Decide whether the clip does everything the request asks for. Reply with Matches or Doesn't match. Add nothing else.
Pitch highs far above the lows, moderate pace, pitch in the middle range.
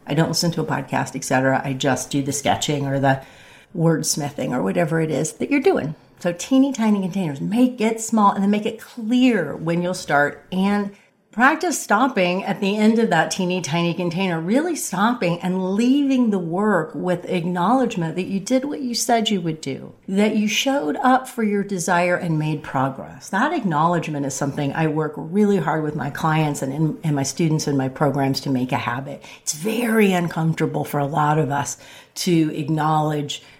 Matches